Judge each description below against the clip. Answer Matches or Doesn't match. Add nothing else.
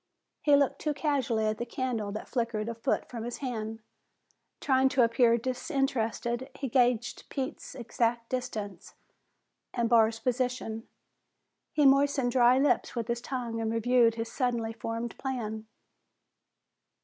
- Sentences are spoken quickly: Doesn't match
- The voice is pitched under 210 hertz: Doesn't match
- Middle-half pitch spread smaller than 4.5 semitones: Matches